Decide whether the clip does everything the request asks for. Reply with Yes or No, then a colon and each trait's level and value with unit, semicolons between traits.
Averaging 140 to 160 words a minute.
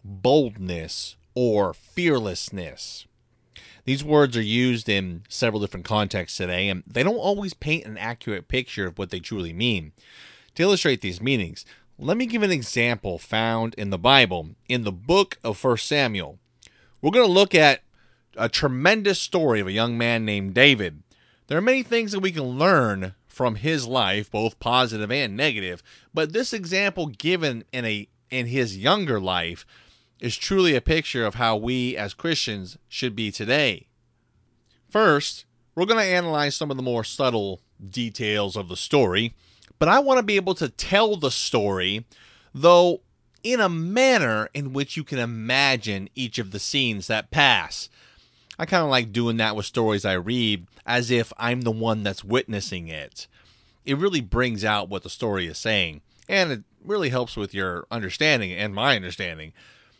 No: average, 170 wpm